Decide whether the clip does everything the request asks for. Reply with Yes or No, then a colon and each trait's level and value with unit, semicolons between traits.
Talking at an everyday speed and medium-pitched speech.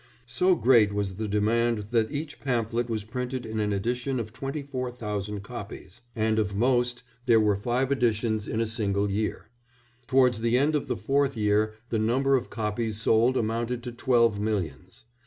No: average, 175 wpm; low, 115 Hz